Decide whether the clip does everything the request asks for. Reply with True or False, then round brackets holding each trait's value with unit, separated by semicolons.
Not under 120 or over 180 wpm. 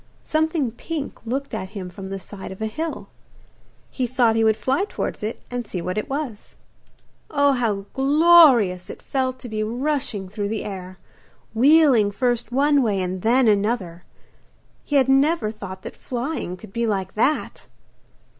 True (170 wpm)